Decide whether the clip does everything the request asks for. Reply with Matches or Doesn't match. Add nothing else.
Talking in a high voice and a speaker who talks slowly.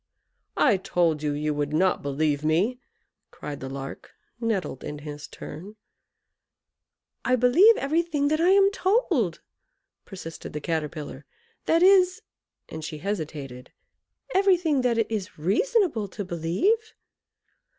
Matches